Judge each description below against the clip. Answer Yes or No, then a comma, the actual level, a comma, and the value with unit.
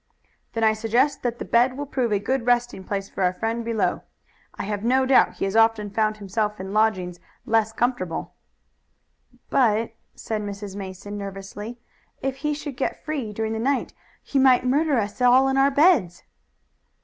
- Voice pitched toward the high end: Yes, high, 225 Hz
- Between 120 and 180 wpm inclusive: Yes, average, 175 wpm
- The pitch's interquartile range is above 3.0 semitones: Yes, average, 3.9 semitones